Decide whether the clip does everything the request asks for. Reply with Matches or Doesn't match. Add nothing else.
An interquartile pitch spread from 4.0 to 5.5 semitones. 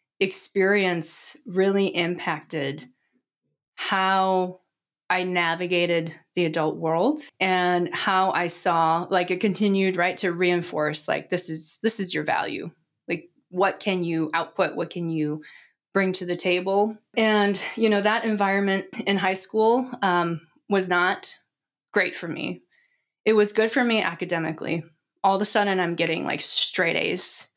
Doesn't match